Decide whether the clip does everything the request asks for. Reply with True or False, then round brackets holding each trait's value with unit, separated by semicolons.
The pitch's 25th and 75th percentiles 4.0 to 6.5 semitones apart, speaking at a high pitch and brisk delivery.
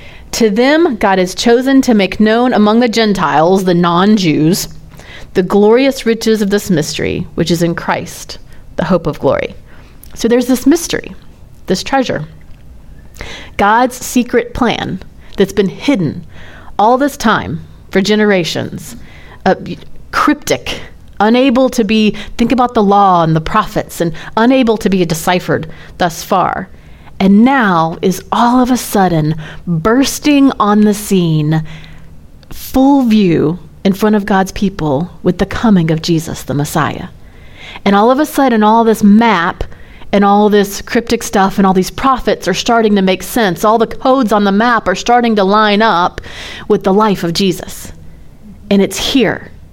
False (4.8 semitones; 205 Hz; 155 wpm)